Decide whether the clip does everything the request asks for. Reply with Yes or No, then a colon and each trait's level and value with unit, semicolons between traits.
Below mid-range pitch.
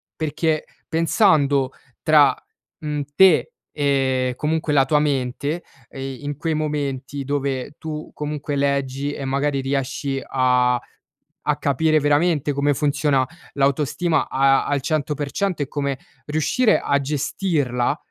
No: medium, 145 Hz